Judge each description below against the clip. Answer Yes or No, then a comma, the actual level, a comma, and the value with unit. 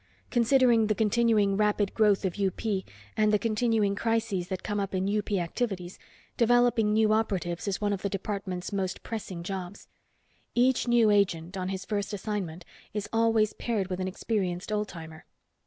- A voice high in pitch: Yes, high, 205 Hz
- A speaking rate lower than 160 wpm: No, average, 165 wpm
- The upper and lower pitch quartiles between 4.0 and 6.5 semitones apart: No, average, 2.8 semitones